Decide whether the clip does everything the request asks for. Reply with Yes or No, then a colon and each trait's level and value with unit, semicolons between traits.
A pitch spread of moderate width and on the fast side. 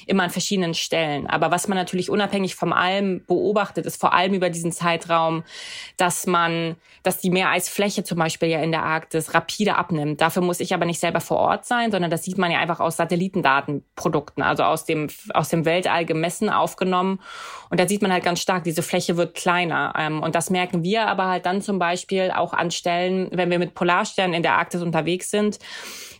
No: narrow, 2.1 semitones; fast, 200 wpm